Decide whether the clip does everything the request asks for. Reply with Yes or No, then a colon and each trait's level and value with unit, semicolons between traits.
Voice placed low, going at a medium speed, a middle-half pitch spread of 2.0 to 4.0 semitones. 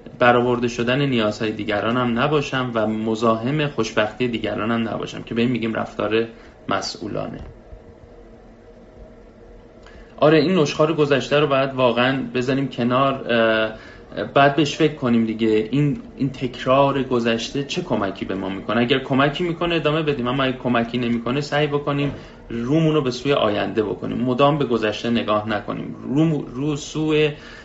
Yes: low, 125 Hz; average, 145 wpm; average, 3.7 semitones